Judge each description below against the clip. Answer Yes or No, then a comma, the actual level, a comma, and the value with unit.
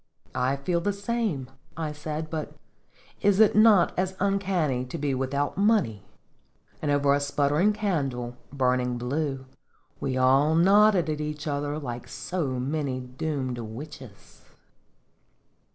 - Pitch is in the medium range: Yes, medium, 145 Hz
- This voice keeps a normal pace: No, slow, 130 wpm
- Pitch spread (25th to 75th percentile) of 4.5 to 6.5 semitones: Yes, average, 5.2 semitones